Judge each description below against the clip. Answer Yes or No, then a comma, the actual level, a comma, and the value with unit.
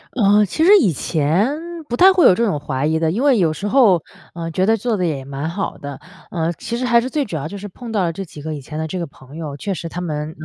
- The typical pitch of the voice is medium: Yes, medium, 175 Hz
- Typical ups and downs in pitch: No, wide, 6.2 semitones